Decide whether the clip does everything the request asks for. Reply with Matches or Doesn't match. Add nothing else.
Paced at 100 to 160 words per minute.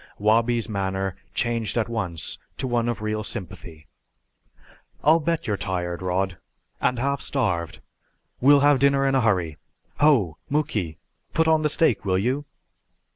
Matches